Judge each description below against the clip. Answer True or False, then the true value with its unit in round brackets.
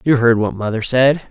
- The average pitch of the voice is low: True (120 Hz)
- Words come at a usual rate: False (230 wpm)